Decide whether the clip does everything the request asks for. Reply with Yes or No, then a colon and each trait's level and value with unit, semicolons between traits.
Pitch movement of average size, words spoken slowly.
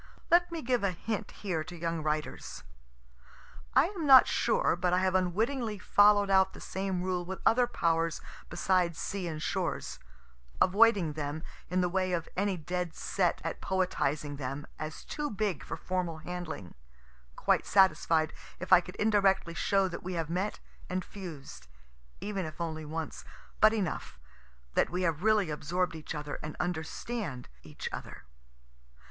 No: average, 3.9 semitones; average, 160 wpm